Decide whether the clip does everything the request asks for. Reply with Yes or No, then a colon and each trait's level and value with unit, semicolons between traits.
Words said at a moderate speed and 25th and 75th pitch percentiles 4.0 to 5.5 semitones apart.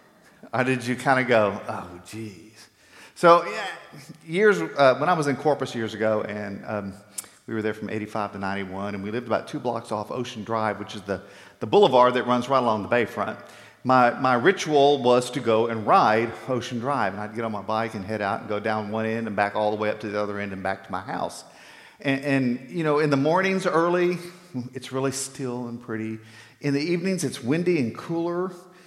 No: fast, 220 wpm; average, 4.6 semitones